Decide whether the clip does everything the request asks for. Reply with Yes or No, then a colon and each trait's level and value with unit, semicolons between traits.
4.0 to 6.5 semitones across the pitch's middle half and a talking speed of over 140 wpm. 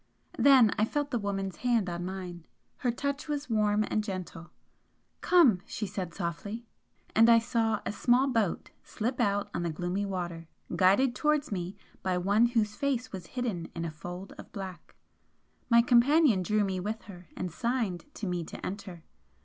Yes: average, 4.7 semitones; average, 175 wpm